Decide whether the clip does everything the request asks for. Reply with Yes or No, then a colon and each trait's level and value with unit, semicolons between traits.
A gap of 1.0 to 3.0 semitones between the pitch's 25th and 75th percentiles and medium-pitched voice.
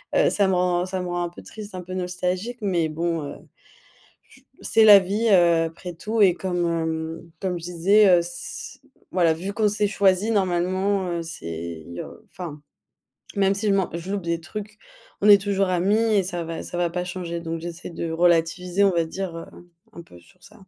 Yes: narrow, 2.6 semitones; medium, 180 Hz